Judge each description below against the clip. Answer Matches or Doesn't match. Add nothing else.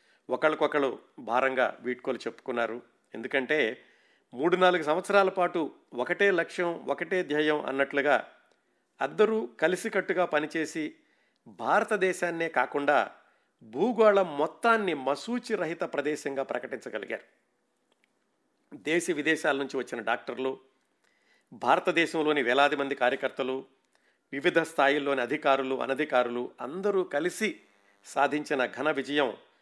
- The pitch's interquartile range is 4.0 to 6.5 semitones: Matches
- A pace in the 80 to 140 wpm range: Matches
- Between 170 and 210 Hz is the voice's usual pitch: Doesn't match